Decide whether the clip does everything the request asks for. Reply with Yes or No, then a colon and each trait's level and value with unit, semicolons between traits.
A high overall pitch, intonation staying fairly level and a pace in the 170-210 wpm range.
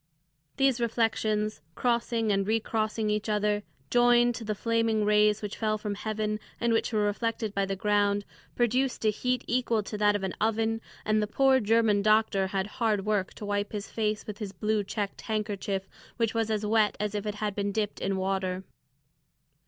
Yes: high, 215 Hz; narrow, 1.6 semitones; average, 185 wpm